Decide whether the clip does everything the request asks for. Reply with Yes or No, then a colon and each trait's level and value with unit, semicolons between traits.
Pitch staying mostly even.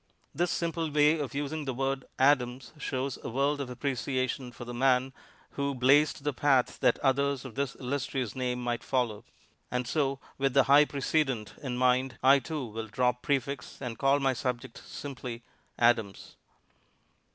Yes: narrow, 2.2 semitones